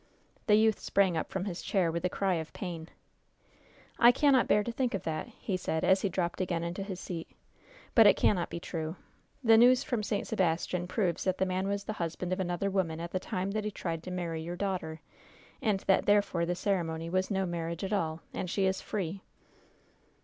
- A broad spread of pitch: No, average, 2.9 semitones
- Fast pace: Yes, fast, 215 wpm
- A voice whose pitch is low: No, medium, 185 Hz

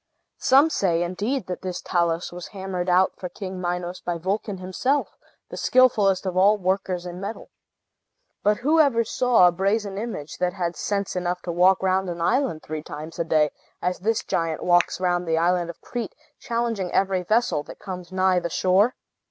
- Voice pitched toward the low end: No, medium, 185 Hz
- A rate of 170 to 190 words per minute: Yes, average, 185 wpm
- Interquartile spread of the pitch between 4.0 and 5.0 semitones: No, average, 2.9 semitones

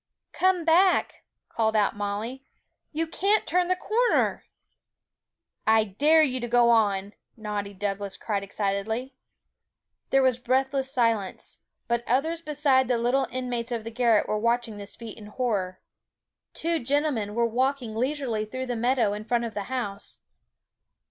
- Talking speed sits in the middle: Yes, average, 150 wpm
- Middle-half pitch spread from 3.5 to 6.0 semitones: Yes, average, 4.1 semitones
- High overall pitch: Yes, high, 235 Hz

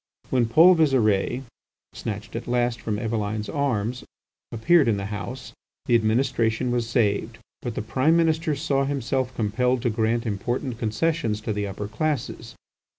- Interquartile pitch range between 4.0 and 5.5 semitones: No, average, 3.6 semitones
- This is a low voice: Yes, low, 120 Hz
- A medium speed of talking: Yes, average, 150 wpm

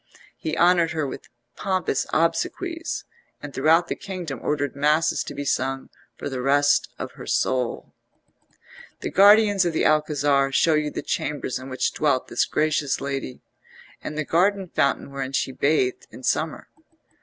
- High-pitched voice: No, medium, 150 Hz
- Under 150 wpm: No, average, 155 wpm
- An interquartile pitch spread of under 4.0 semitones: Yes, average, 3.4 semitones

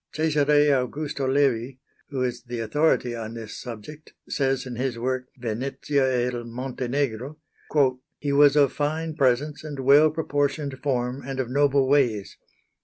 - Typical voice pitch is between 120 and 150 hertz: Yes, low, 135 Hz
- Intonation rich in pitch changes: No, average, 2.8 semitones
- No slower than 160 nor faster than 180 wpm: No, average, 145 wpm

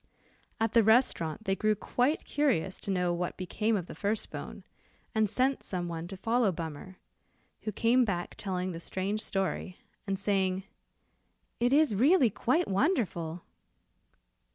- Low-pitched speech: No, high, 200 Hz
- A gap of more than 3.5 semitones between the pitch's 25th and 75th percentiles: Yes, average, 4.3 semitones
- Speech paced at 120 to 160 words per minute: Yes, average, 150 wpm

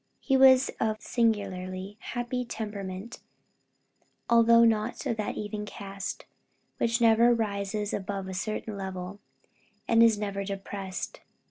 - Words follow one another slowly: Yes, slow, 125 wpm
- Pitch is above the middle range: Yes, high, 210 Hz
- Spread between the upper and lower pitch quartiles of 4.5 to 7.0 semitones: No, average, 2.7 semitones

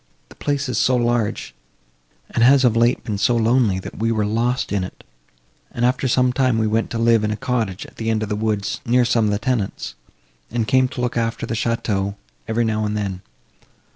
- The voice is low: Yes, low, 115 Hz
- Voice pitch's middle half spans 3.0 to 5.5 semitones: No, narrow, 2.5 semitones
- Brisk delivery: Yes, fast, 220 wpm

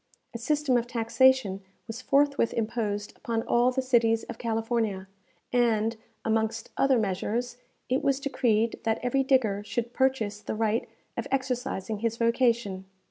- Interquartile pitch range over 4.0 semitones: No, narrow, 2.5 semitones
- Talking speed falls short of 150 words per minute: Yes, average, 140 wpm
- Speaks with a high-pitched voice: Yes, high, 230 Hz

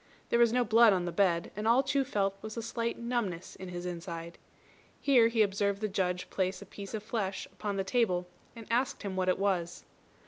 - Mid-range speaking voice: No, high, 200 Hz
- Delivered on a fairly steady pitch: No, average, 3.9 semitones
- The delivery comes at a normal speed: No, fast, 215 wpm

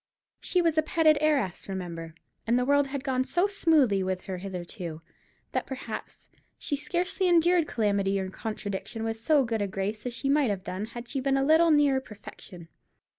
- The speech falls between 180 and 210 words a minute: Yes, average, 185 wpm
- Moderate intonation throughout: No, wide, 7.4 semitones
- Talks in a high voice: Yes, high, 245 Hz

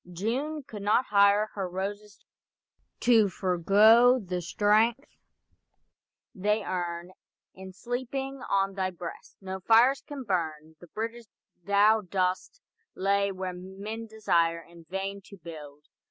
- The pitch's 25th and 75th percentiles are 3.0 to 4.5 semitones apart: Yes, average, 3.4 semitones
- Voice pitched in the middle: No, high, 200 Hz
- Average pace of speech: No, slow, 125 wpm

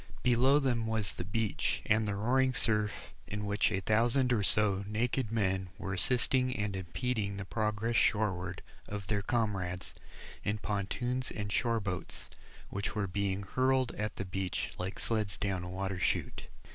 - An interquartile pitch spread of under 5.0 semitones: Yes, average, 3.2 semitones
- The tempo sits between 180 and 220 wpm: No, average, 160 wpm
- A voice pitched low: Yes, low, 105 Hz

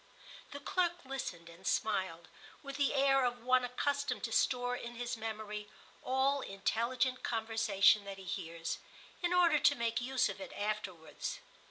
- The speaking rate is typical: Yes, average, 155 wpm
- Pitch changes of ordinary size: Yes, average, 4.5 semitones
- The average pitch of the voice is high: Yes, high, 240 Hz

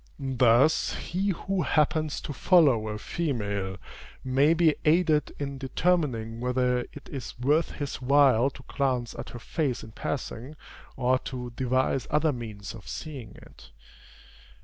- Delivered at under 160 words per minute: Yes, average, 140 wpm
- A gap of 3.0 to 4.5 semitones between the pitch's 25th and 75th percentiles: Yes, average, 4.0 semitones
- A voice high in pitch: No, low, 130 Hz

